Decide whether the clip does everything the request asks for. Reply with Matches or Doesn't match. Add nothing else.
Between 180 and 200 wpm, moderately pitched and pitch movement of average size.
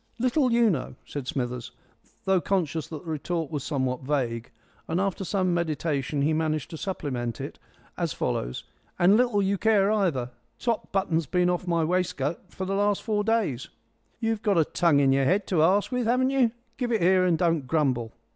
Doesn't match